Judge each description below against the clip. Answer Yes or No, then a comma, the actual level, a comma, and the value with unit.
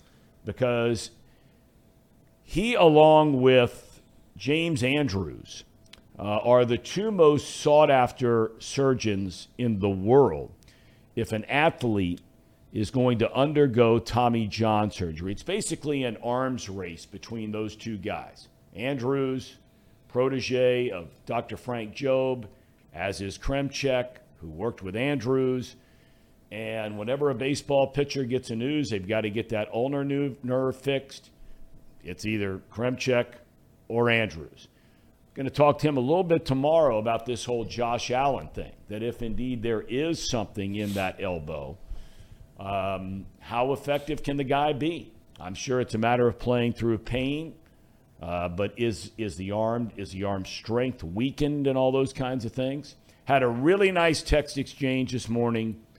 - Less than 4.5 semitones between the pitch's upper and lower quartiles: Yes, average, 3.7 semitones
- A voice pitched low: Yes, low, 120 Hz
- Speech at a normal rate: Yes, average, 145 wpm